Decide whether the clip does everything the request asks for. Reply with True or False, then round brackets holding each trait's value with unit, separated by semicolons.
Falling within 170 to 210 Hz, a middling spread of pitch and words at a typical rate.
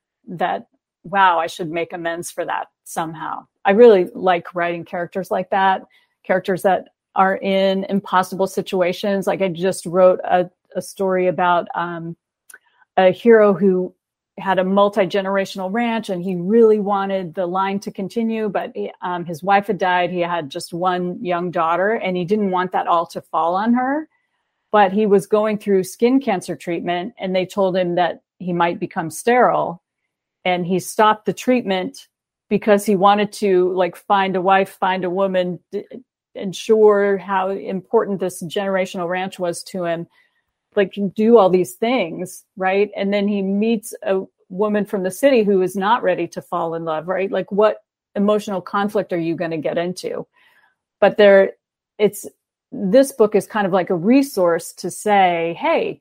False (190 Hz; 2.2 semitones; 170 wpm)